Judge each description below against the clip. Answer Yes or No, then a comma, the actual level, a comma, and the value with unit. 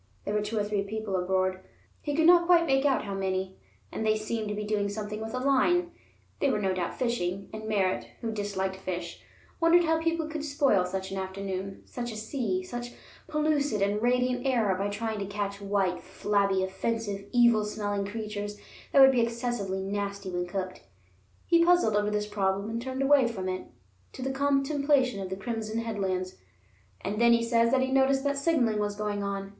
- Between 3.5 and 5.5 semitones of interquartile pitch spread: Yes, average, 4.5 semitones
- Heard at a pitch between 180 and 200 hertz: No, high, 215 Hz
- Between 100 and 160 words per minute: No, average, 195 wpm